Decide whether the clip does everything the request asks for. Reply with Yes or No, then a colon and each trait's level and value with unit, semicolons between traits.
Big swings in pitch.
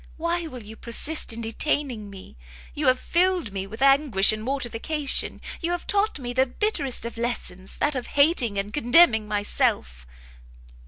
Yes: wide, 5.8 semitones